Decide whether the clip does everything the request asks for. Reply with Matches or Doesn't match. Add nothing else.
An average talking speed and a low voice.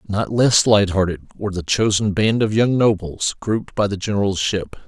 Matches